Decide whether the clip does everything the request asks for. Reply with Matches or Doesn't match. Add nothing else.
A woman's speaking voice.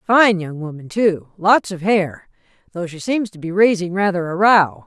Matches